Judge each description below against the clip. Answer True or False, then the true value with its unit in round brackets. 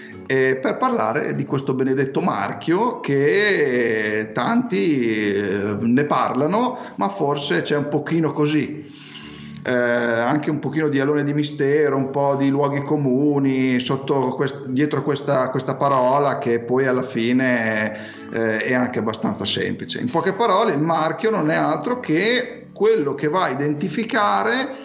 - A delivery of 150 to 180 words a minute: False (140 wpm)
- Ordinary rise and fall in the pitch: True (3.2 semitones)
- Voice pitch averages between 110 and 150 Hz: True (140 Hz)